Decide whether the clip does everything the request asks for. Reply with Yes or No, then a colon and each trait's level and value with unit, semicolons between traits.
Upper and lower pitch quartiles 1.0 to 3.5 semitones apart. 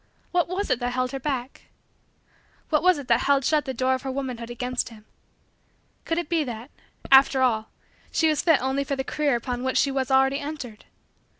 Yes: average, 2.8 semitones